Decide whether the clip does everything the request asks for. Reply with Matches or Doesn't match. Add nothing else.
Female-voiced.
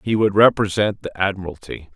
Doesn't match